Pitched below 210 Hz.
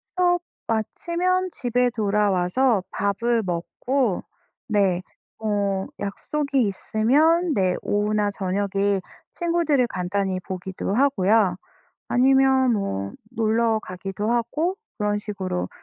No: high, 215 Hz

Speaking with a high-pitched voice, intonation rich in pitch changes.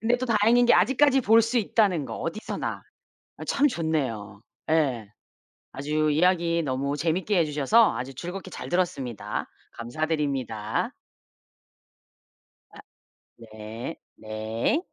No: medium, 160 Hz; wide, 8.3 semitones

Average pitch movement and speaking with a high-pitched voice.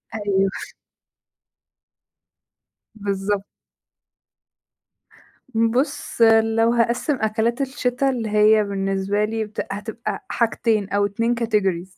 No: narrow, 2.3 semitones; high, 220 Hz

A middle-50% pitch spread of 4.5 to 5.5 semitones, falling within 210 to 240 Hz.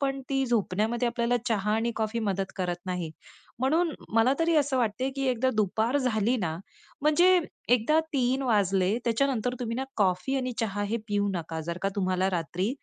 Yes: average, 5.1 semitones; high, 225 Hz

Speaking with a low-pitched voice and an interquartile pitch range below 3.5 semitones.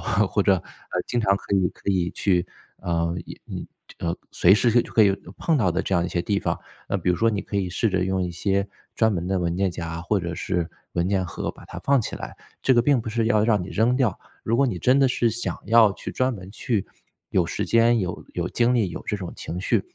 No: low, 100 Hz; average, 4.3 semitones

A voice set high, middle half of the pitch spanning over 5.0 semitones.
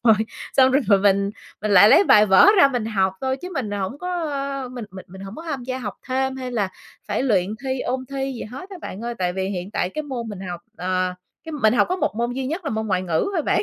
Yes: high, 230 Hz; wide, 5.5 semitones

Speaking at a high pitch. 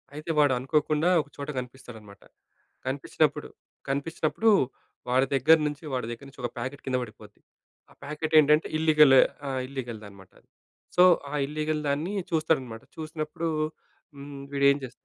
No: medium, 140 Hz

